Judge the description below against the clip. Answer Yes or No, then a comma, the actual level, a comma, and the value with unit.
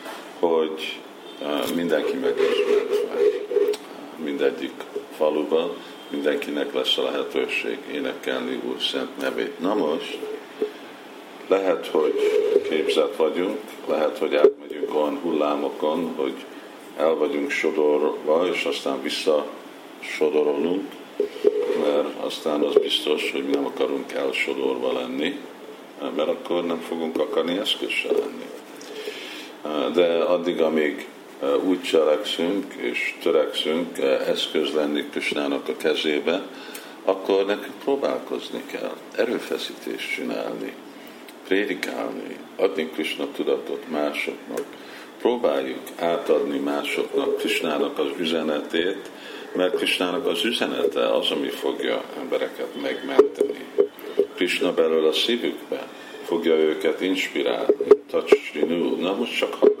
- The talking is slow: Yes, slow, 100 wpm